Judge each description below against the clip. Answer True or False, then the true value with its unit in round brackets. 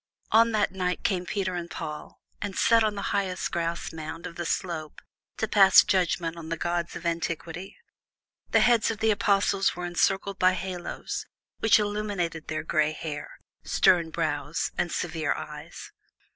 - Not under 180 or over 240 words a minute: False (160 wpm)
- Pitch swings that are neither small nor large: True (3.2 semitones)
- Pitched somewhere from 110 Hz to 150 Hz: False (175 Hz)